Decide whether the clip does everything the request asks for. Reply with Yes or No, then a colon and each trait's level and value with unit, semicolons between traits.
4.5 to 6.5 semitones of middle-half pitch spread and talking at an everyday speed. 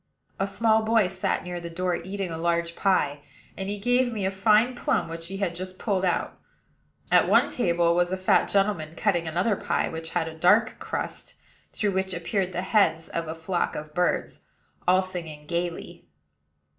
No: average, 2.8 semitones; average, 185 wpm